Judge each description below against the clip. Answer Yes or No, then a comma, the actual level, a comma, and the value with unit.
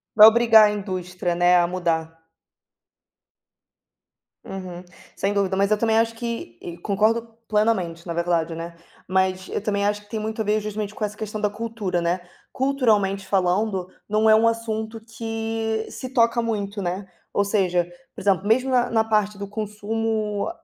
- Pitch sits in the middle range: No, high, 210 Hz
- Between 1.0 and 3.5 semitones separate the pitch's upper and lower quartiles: Yes, average, 3.0 semitones